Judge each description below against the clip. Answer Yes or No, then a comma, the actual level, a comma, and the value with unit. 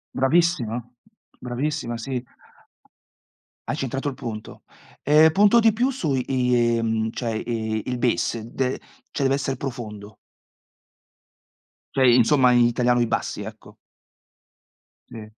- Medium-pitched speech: No, low, 125 Hz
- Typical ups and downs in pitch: Yes, average, 3.1 semitones